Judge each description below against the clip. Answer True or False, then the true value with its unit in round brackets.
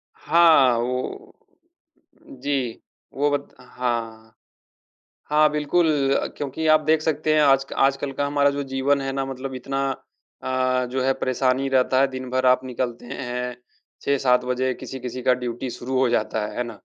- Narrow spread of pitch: True (2.1 semitones)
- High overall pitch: False (130 Hz)